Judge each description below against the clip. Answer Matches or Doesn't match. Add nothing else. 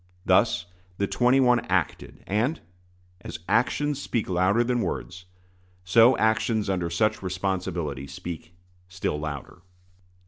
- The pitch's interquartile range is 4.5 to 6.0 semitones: Matches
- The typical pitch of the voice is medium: Doesn't match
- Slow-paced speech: Matches